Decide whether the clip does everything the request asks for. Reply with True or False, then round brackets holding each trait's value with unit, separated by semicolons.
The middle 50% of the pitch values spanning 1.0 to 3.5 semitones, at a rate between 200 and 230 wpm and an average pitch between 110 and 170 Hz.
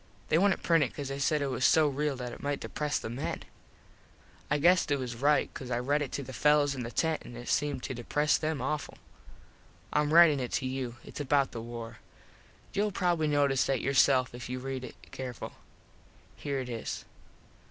True (2.9 semitones; 205 wpm; 140 Hz)